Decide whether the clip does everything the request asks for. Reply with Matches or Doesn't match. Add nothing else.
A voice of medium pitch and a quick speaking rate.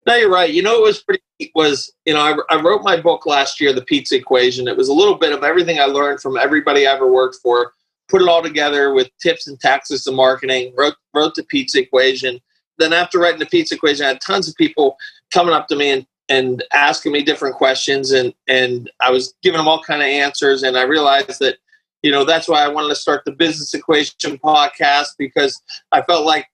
Matches